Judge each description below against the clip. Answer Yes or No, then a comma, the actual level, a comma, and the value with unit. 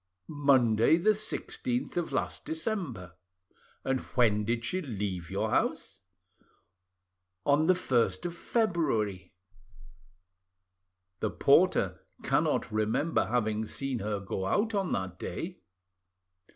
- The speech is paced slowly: Yes, slow, 110 wpm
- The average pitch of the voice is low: Yes, low, 125 Hz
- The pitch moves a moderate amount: No, wide, 7.9 semitones